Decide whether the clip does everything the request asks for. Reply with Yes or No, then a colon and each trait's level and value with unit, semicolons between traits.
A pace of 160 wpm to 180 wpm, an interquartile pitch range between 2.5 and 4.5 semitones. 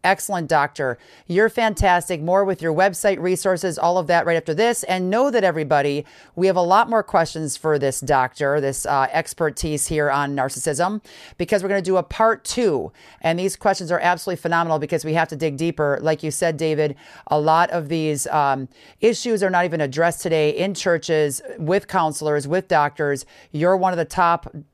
No: average, 195 wpm; average, 3.6 semitones